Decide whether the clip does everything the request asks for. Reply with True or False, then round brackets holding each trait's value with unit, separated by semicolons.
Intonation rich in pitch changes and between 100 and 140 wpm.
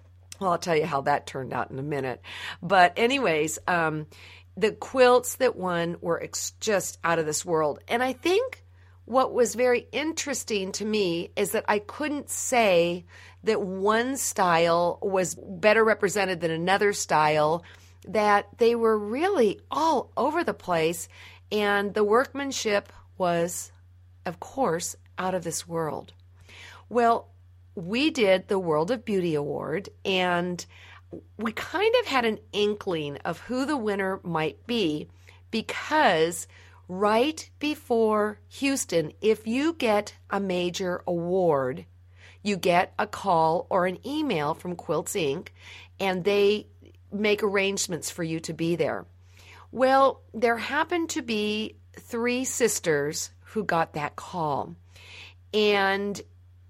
True (8.0 semitones; 135 wpm)